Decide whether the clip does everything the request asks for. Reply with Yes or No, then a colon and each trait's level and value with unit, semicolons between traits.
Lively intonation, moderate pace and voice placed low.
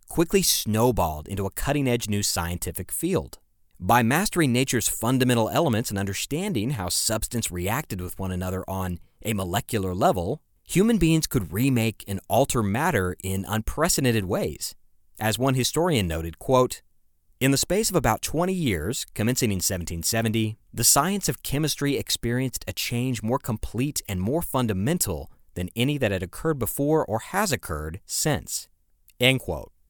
Yes: wide, 5.9 semitones; average, 150 wpm; low, 110 Hz